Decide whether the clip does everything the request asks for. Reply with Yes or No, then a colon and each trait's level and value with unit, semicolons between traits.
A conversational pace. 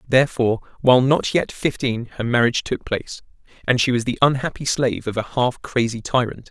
Yes: average, 185 wpm